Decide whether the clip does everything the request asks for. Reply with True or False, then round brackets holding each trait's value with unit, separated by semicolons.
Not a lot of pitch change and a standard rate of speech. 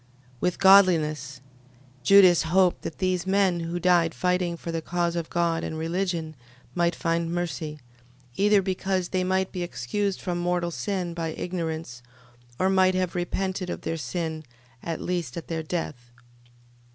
True (2.1 semitones; 150 wpm)